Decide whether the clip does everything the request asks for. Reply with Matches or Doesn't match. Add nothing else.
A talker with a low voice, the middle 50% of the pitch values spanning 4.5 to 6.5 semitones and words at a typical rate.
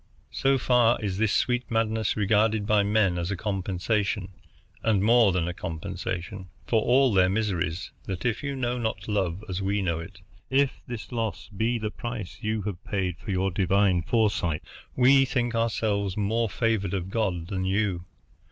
Doesn't match